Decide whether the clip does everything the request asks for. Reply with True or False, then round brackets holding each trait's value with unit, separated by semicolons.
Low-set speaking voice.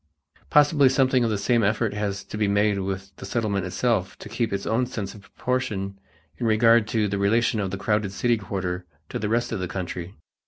True (105 Hz)